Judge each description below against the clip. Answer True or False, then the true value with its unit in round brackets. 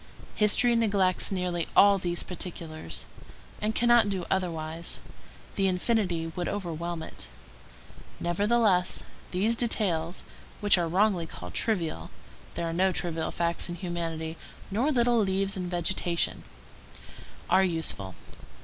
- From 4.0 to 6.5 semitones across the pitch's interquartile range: False (3.4 semitones)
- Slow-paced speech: True (115 wpm)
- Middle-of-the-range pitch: True (180 Hz)